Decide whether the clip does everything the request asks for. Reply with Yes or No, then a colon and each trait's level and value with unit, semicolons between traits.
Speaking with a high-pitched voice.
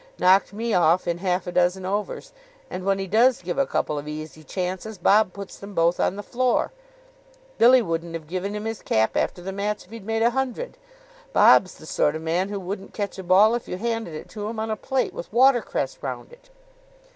Yes: high, 195 Hz